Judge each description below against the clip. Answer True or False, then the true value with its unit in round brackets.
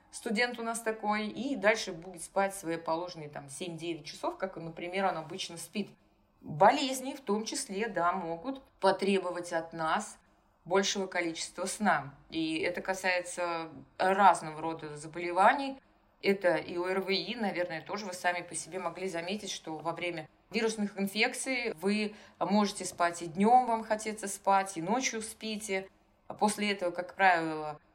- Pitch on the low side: False (190 Hz)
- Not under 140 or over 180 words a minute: True (145 wpm)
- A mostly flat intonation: False (3.7 semitones)